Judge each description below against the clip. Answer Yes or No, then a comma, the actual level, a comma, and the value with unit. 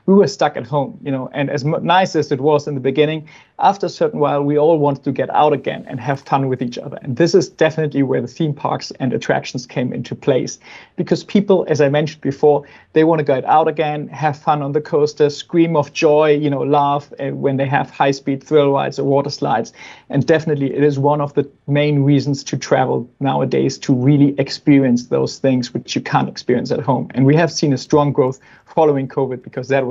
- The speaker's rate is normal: No, fast, 225 wpm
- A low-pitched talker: No, medium, 145 Hz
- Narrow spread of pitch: Yes, narrow, 1.9 semitones